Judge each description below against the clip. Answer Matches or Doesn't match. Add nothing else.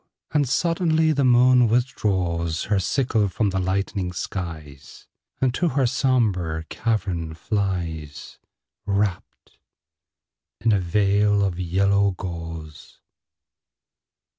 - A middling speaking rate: Doesn't match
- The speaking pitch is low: Matches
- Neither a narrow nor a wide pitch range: Doesn't match